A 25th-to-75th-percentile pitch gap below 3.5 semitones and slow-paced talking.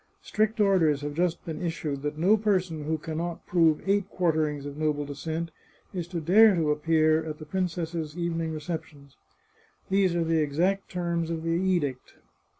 No: narrow, 2.6 semitones; average, 170 wpm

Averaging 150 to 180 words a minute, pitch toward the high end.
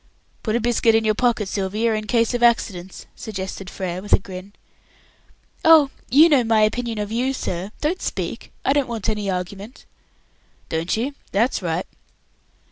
Yes: average, 165 wpm; high, 220 Hz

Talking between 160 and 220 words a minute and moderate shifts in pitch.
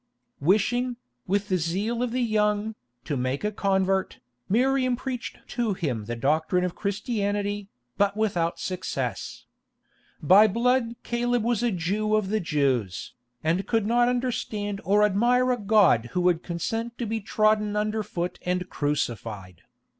No: average, 145 wpm; average, 4.8 semitones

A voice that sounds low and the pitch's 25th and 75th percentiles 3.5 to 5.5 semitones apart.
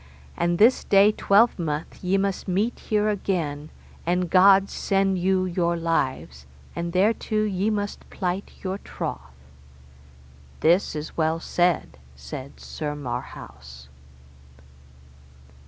No: medium, 180 Hz; average, 4.2 semitones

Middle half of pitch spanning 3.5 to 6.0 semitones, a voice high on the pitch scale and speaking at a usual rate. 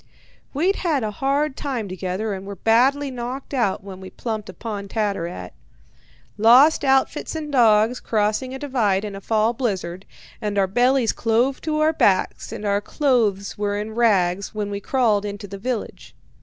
Yes: average, 4.5 semitones; high, 220 Hz; average, 170 wpm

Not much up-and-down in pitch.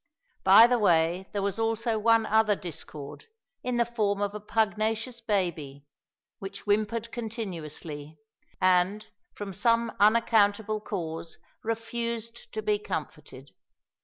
No: average, 3.3 semitones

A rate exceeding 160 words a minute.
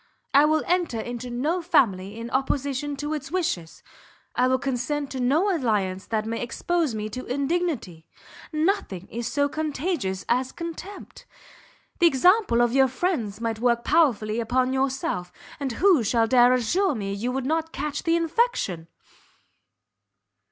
No: average, 150 wpm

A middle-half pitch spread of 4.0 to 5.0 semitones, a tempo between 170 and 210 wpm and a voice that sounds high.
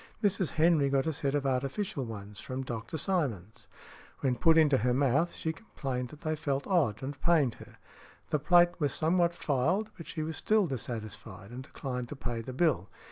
No: average, 4.7 semitones; average, 190 wpm; medium, 140 Hz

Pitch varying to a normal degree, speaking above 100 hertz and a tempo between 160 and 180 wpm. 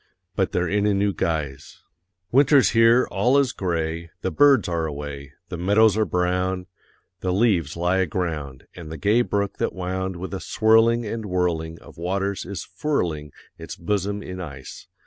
No: average, 3.7 semitones; very low, 95 Hz; average, 165 wpm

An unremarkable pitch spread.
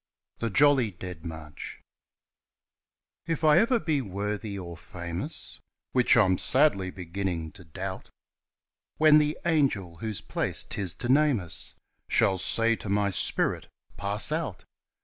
No: wide, 7.7 semitones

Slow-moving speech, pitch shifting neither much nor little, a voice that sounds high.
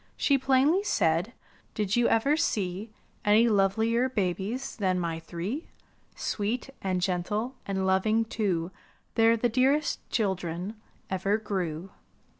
Yes: slow, 120 wpm; average, 4.2 semitones; high, 210 Hz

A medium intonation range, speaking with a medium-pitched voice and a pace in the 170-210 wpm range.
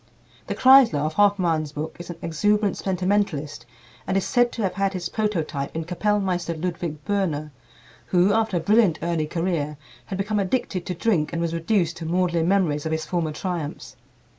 Yes: average, 3.9 semitones; medium, 175 Hz; average, 175 wpm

